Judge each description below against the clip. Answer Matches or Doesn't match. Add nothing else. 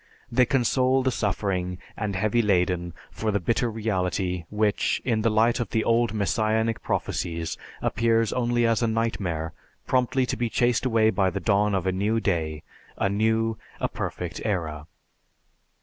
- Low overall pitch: Matches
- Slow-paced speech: Doesn't match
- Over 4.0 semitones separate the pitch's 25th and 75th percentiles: Doesn't match